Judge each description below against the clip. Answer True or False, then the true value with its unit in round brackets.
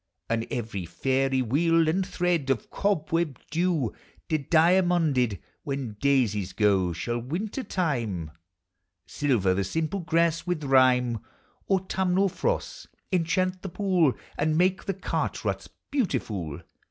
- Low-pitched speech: False (155 Hz)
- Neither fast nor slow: False (115 wpm)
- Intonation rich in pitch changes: True (7.0 semitones)